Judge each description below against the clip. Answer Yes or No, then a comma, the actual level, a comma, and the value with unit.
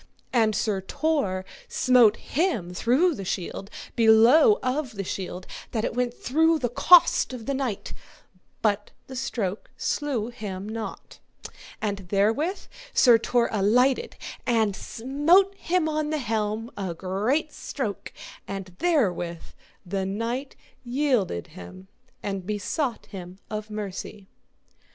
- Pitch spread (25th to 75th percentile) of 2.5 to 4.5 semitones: No, wide, 5.6 semitones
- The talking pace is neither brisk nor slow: No, slow, 125 wpm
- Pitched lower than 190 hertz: No, high, 225 Hz